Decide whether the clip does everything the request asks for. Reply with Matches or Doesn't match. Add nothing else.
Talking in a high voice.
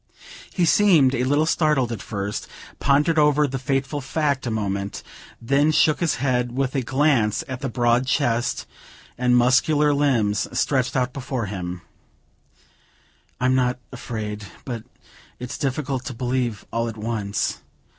Doesn't match